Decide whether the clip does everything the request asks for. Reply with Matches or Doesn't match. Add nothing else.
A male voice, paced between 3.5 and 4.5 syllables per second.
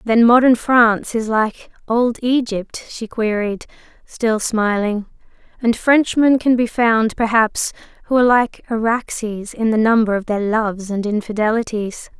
Doesn't match